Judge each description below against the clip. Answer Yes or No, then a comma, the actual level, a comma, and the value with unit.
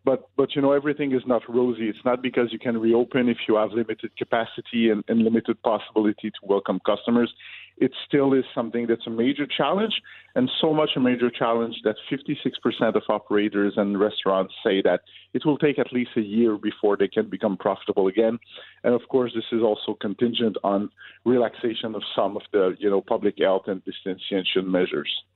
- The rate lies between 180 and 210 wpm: Yes, average, 190 wpm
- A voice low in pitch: Yes, low, 115 Hz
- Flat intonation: No, average, 3.0 semitones